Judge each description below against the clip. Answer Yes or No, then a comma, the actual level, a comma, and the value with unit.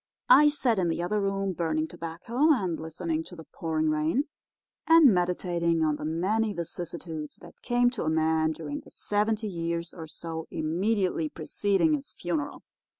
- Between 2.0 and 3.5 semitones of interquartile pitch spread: No, average, 4.6 semitones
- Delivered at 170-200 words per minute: No, average, 160 wpm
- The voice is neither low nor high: Yes, medium, 170 Hz